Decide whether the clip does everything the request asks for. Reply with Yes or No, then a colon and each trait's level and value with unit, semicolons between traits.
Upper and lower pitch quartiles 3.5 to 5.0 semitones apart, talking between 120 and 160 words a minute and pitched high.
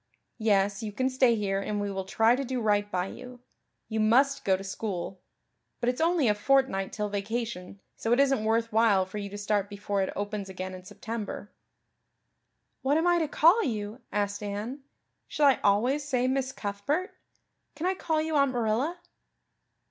No: average, 4.7 semitones; average, 185 wpm; high, 220 Hz